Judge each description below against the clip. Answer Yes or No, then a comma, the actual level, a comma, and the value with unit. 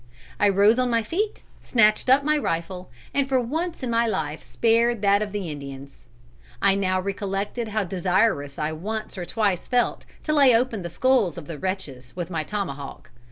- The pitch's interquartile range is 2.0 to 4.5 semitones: No, average, 5.3 semitones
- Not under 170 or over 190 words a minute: Yes, average, 180 wpm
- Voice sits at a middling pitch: No, high, 200 Hz